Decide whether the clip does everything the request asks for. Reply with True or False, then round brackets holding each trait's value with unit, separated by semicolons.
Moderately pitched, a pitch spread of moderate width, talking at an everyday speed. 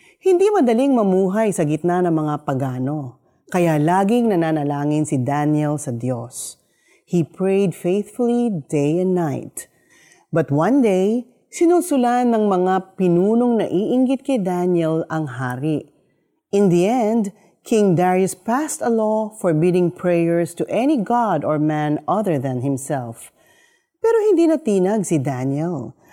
False (180 Hz; 7.0 semitones; 130 wpm)